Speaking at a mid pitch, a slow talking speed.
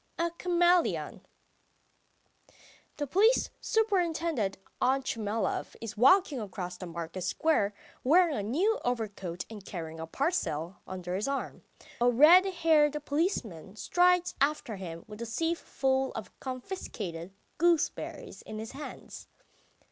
No: very high, 255 Hz; slow, 120 wpm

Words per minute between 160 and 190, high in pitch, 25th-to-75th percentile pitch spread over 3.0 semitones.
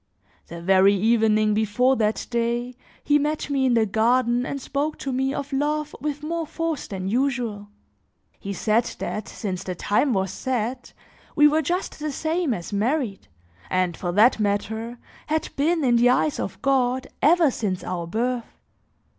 Yes: average, 165 wpm; high, 245 Hz; average, 5.2 semitones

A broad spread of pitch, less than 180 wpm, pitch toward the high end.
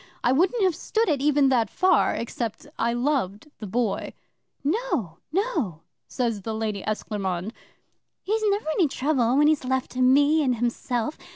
Yes: wide, 5.7 semitones; average, 160 wpm; very high, 255 Hz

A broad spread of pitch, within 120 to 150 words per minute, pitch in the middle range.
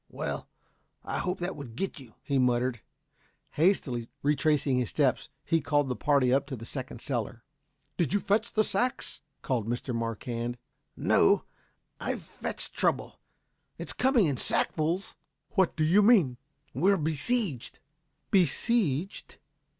Yes: wide, 7.4 semitones; average, 140 wpm; medium, 145 Hz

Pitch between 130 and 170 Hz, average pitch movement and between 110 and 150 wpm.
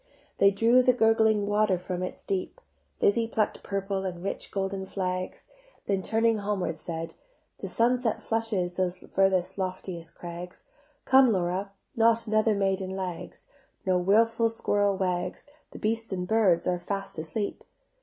No: high, 195 Hz; average, 3.3 semitones; average, 145 wpm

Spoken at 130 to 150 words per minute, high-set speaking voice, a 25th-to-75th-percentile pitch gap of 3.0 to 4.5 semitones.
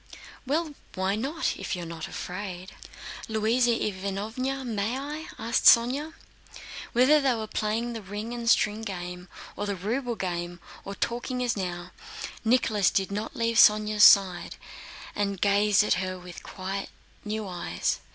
Yes: average, 145 wpm; high, 210 Hz; average, 3.9 semitones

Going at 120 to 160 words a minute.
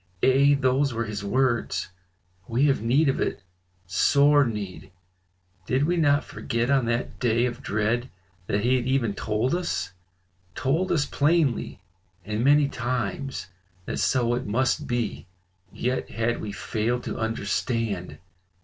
Yes: average, 140 wpm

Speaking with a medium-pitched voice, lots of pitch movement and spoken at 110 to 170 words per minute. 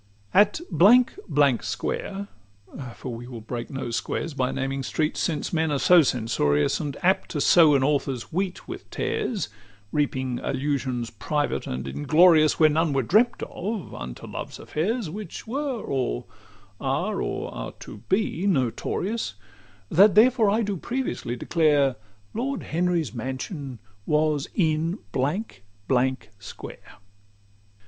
Yes: medium, 150 Hz; wide, 6.8 semitones; average, 140 wpm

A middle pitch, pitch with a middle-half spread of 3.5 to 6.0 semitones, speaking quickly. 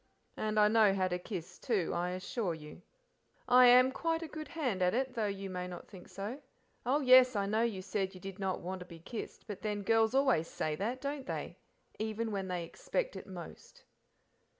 No: high, 210 Hz; average, 5.2 semitones; fast, 210 wpm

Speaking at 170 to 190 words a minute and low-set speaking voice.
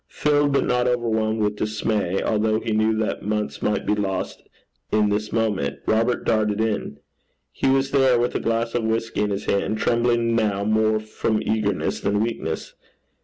Yes: average, 175 wpm; low, 110 Hz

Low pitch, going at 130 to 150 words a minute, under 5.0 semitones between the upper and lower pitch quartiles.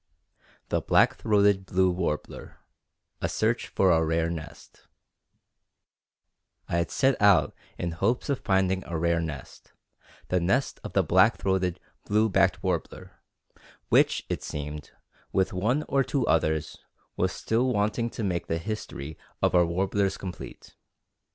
Yes: very low, 95 Hz; average, 140 wpm; average, 3.6 semitones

